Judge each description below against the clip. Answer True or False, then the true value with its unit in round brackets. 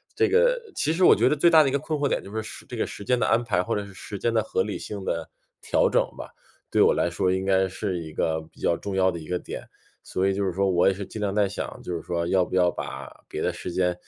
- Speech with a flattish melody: False (3.7 semitones)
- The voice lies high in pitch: False (95 Hz)